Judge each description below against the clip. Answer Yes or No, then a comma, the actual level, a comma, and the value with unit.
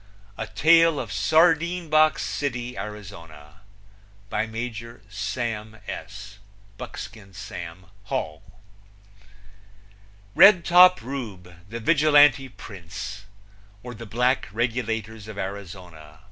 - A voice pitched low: Yes, low, 110 Hz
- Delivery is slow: Yes, slow, 90 wpm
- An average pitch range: No, wide, 5.7 semitones